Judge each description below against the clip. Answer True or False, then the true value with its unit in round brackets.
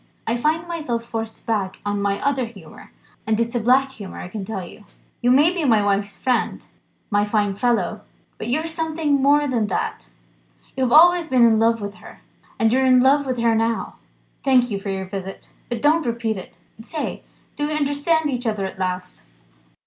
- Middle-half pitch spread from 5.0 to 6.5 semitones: True (5.4 semitones)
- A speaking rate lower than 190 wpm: False (195 wpm)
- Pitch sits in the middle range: False (235 Hz)